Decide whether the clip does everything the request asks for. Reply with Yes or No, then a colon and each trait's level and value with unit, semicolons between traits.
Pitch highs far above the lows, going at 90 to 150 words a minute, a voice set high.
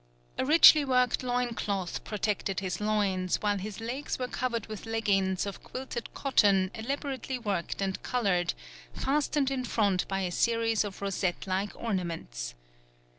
No: average, 4.5 semitones; average, 145 wpm; high, 210 Hz